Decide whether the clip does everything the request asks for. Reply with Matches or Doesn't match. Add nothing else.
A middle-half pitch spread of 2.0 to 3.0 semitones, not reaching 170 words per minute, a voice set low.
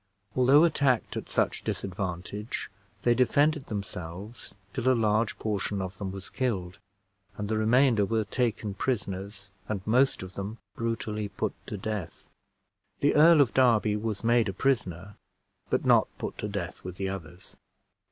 Doesn't match